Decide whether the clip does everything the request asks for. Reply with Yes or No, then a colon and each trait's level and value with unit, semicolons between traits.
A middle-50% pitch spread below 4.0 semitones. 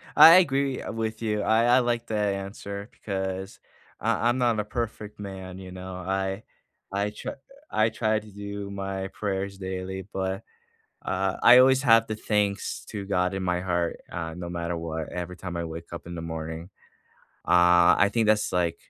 Yes: average, 3.0 semitones